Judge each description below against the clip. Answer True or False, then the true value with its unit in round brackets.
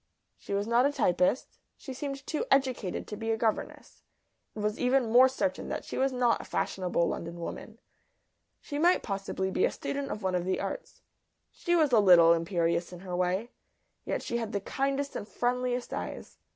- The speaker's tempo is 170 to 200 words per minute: True (190 wpm)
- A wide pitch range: True (6.2 semitones)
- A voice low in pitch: False (225 Hz)